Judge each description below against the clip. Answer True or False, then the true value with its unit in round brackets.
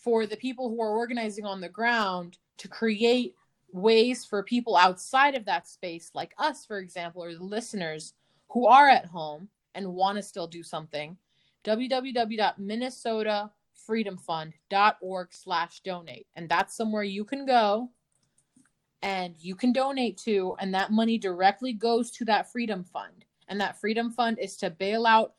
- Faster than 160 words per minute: False (155 wpm)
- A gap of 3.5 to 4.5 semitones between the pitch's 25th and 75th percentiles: True (4.2 semitones)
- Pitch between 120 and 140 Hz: False (210 Hz)